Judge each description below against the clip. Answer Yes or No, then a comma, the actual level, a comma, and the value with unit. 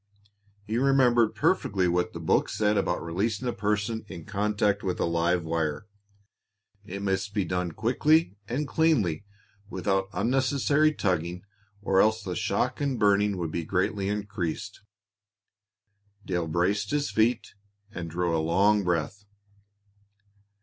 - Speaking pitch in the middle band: No, low, 100 Hz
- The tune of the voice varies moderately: Yes, average, 3.7 semitones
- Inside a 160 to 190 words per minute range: No, slow, 135 wpm